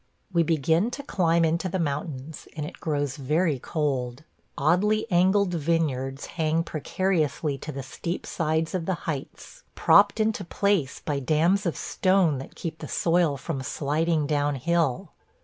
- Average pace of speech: Yes, average, 150 wpm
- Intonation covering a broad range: No, average, 3.5 semitones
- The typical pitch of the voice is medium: Yes, medium, 160 Hz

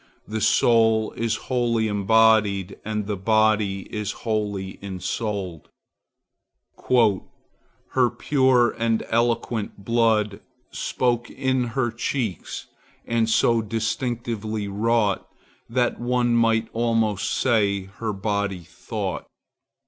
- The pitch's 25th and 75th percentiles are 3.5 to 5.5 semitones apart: No, narrow, 2.5 semitones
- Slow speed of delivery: Yes, slow, 95 wpm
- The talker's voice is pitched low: Yes, low, 110 Hz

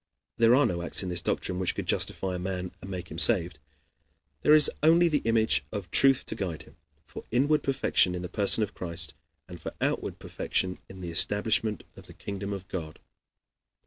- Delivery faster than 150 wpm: Yes, average, 200 wpm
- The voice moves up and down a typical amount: Yes, average, 4.3 semitones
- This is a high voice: No, very low, 95 Hz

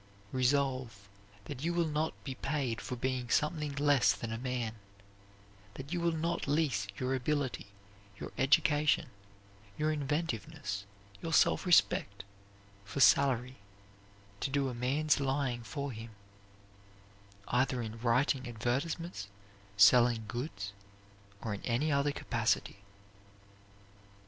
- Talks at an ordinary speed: No, slow, 120 wpm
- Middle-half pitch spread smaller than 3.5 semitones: No, average, 3.9 semitones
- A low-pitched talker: Yes, low, 130 Hz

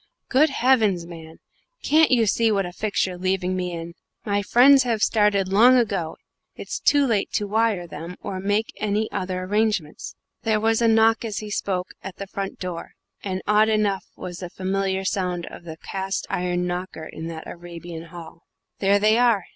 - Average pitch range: Yes, average, 3.5 semitones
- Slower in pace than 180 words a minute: No, average, 185 wpm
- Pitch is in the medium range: No, high, 195 Hz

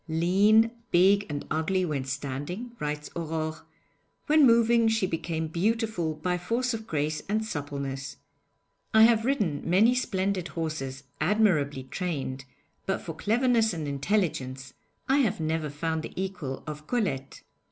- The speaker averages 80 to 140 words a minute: Yes, slow, 135 wpm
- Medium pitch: Yes, medium, 170 Hz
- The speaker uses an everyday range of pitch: No, wide, 6.6 semitones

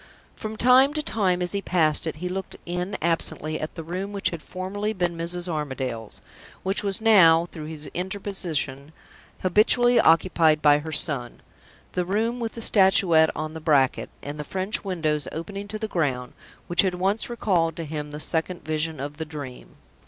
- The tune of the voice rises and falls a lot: No, average, 4.2 semitones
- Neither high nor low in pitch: Yes, medium, 170 Hz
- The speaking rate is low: No, average, 180 wpm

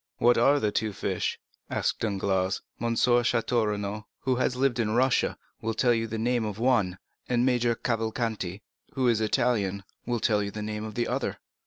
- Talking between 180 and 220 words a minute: Yes, average, 190 wpm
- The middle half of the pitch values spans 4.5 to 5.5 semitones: No, narrow, 2.4 semitones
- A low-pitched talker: Yes, low, 115 Hz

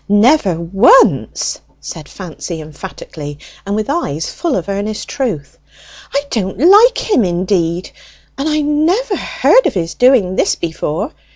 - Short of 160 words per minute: Yes, slow, 135 wpm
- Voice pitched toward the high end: Yes, high, 205 Hz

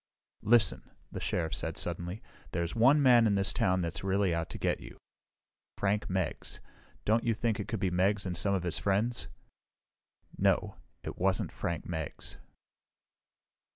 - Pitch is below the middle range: Yes, very low, 95 Hz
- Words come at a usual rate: Yes, average, 155 wpm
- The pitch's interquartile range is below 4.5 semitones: Yes, average, 3.7 semitones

